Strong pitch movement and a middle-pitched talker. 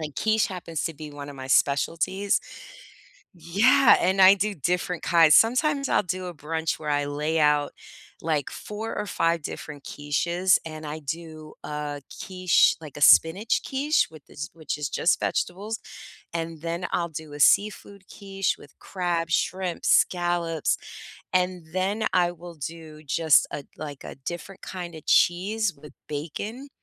No: average, 3.7 semitones; medium, 170 Hz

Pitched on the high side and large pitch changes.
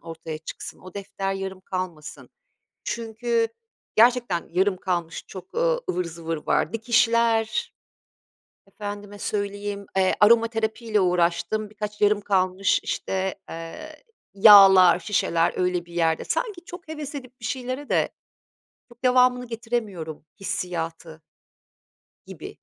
No: high, 205 Hz; average, 4.4 semitones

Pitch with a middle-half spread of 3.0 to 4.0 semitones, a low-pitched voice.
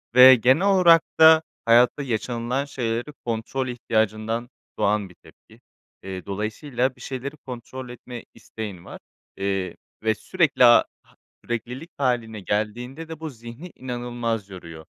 Yes: average, 3.3 semitones; low, 120 Hz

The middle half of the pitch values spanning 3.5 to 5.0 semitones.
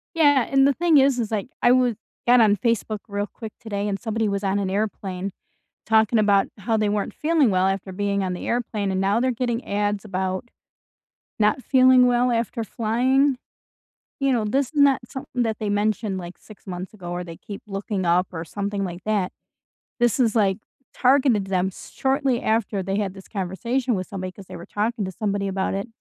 Yes: average, 3.8 semitones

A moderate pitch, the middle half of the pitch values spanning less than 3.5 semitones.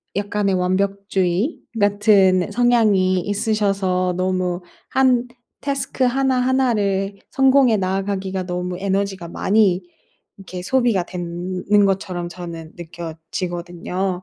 No: high, 195 Hz; narrow, 2.6 semitones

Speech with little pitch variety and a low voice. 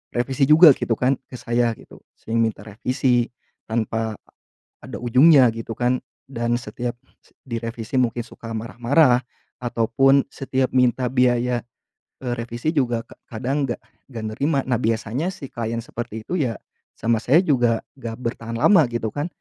Yes: narrow, 2.3 semitones; low, 120 Hz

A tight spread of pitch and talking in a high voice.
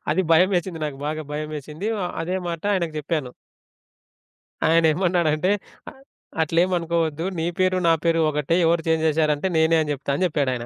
No: narrow, 2.1 semitones; medium, 160 Hz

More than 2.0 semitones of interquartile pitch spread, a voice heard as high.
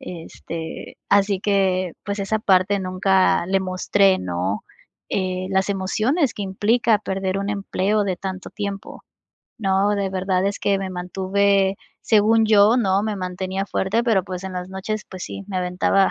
No: narrow, 1.5 semitones; high, 195 Hz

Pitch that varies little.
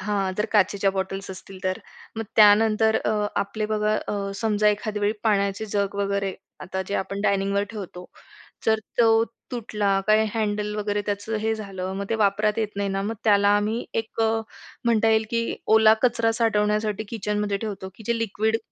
Yes: narrow, 1.7 semitones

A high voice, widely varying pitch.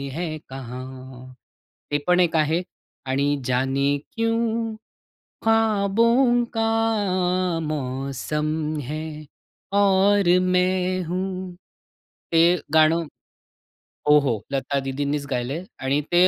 No: medium, 165 Hz; wide, 5.8 semitones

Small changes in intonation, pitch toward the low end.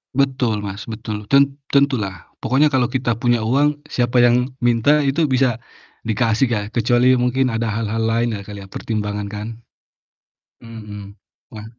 No: average, 3.4 semitones; low, 120 Hz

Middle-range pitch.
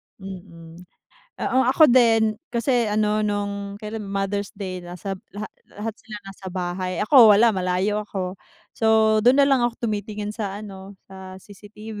No: high, 205 Hz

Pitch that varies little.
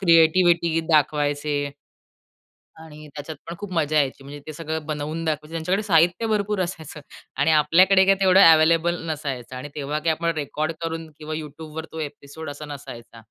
Yes: narrow, 2.2 semitones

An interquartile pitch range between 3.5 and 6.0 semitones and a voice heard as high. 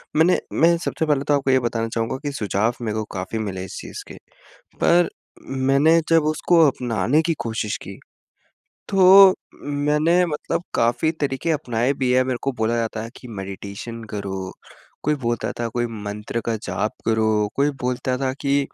No: average, 4.8 semitones; low, 120 Hz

